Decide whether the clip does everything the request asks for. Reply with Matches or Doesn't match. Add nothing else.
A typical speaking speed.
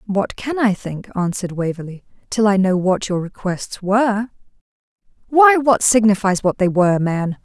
Matches